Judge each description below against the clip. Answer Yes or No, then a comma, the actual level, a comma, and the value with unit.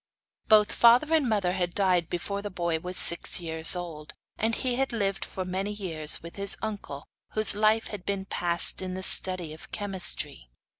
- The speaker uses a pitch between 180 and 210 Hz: Yes, high, 190 Hz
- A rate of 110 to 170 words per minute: No, average, 185 wpm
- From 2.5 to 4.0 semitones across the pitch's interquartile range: Yes, average, 3.3 semitones